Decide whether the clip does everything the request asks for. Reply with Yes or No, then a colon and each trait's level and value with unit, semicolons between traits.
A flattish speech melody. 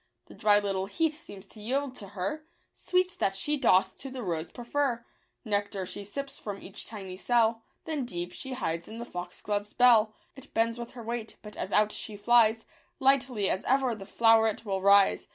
No: average, 3.9 semitones